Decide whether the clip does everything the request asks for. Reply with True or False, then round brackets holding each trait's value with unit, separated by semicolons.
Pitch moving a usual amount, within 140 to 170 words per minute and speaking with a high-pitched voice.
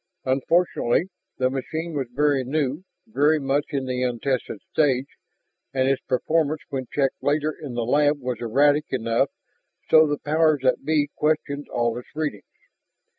False (3.0 semitones; 150 wpm; 140 Hz)